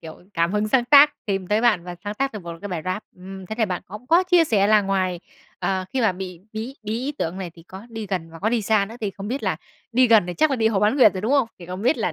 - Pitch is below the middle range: No, high, 210 Hz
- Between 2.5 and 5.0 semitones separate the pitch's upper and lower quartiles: Yes, average, 3.9 semitones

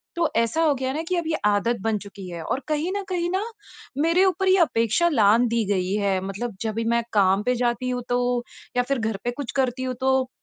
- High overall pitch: Yes, high, 245 Hz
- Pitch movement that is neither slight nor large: No, wide, 6.1 semitones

